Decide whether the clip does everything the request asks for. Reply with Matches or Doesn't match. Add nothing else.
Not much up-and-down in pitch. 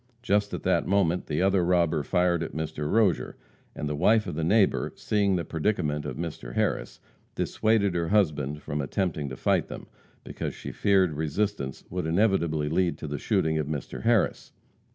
Doesn't match